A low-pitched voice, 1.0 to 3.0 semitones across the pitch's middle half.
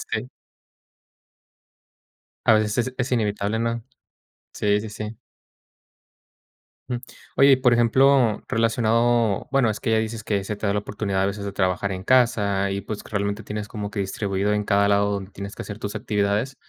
Yes: low, 105 Hz; narrow, 2.4 semitones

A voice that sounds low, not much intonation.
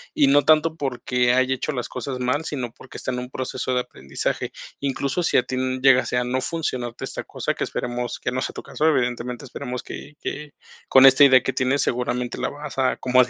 Yes: low, 130 Hz; narrow, 1.9 semitones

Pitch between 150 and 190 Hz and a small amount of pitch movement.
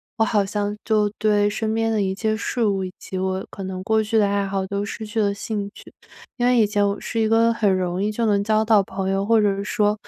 No: high, 205 Hz; narrow, 1.8 semitones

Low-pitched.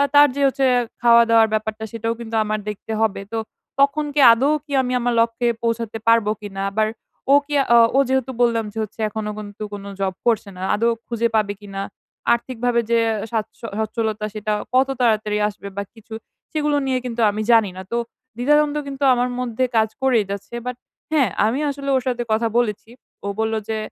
No: high, 230 Hz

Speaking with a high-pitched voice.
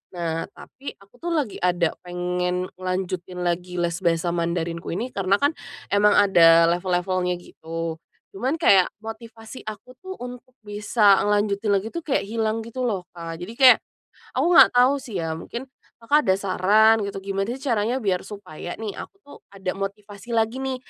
Yes: high, 200 Hz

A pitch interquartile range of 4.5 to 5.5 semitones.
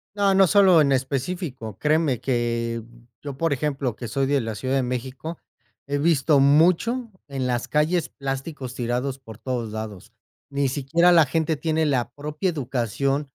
No: average, 4.0 semitones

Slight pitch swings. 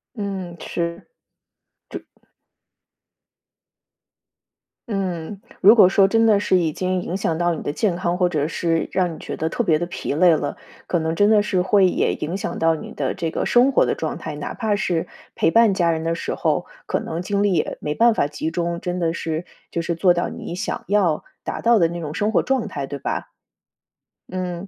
No: average, 3.4 semitones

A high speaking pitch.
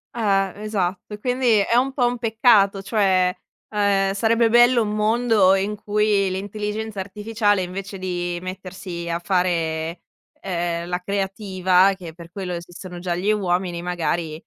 Yes: high, 195 Hz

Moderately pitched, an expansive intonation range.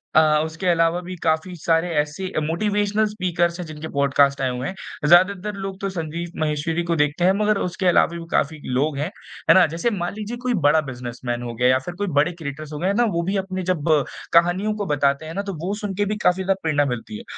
No: medium, 170 Hz; average, 4.3 semitones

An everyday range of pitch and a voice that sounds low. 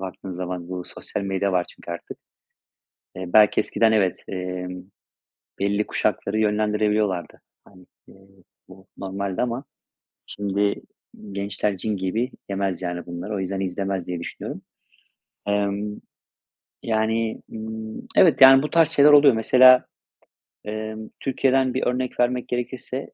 Yes: average, 3.3 semitones; low, 105 Hz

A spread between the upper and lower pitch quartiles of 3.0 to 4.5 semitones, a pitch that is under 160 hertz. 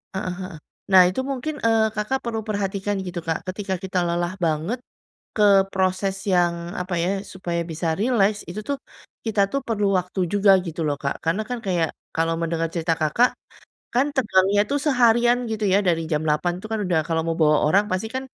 No: average, 4.2 semitones; high, 190 Hz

